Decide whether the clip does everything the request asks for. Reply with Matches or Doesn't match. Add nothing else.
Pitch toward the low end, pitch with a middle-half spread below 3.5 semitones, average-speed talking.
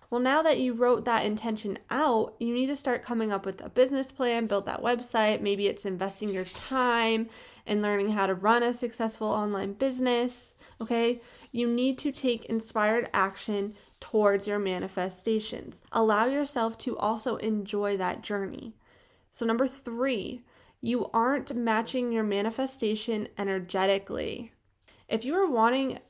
Doesn't match